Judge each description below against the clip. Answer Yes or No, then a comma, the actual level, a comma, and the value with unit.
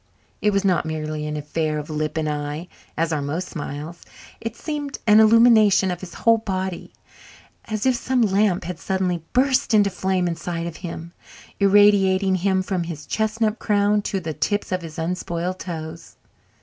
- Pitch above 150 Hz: Yes, medium, 185 Hz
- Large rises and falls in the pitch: No, average, 4.1 semitones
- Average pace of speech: Yes, average, 170 wpm